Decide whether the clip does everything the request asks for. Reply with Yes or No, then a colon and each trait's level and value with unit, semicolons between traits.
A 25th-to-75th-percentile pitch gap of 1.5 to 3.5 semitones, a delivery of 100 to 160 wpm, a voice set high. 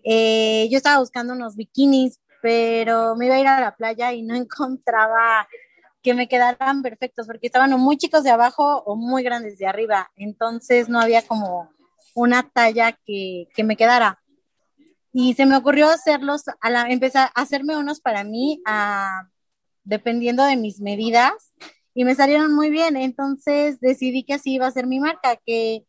No: average, 3.2 semitones; average, 170 wpm; high, 245 Hz